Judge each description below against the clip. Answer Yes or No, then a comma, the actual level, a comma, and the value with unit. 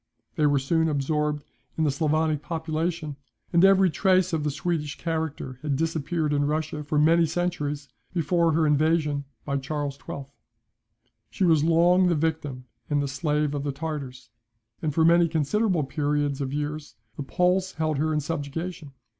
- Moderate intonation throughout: No, narrow, 2.3 semitones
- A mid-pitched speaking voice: Yes, medium, 155 Hz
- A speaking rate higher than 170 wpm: No, average, 165 wpm